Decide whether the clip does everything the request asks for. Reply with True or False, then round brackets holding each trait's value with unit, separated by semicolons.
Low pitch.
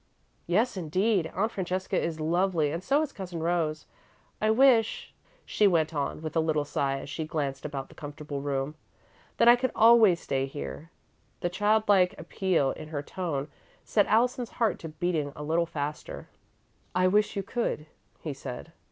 False (170 Hz)